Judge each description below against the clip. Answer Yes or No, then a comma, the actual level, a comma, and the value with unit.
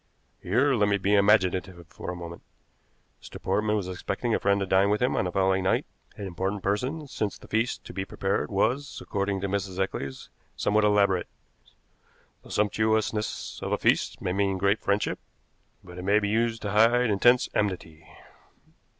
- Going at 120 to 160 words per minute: No, average, 175 wpm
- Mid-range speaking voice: No, low, 100 Hz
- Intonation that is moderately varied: No, narrow, 2.1 semitones